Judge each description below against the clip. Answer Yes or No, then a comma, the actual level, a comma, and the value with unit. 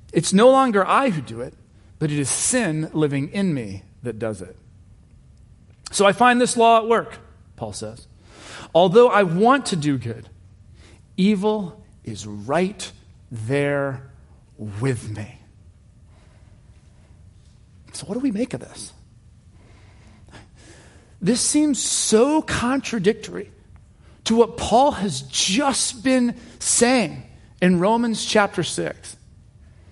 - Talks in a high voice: No, low, 135 Hz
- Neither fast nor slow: No, slow, 120 wpm